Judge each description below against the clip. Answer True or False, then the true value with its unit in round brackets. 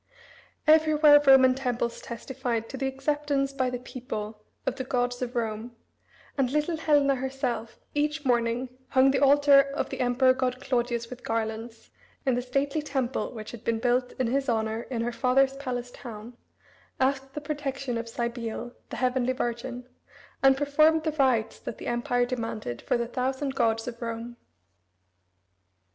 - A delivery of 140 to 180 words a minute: True (160 wpm)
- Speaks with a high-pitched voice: True (255 Hz)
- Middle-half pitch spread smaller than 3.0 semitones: True (2.5 semitones)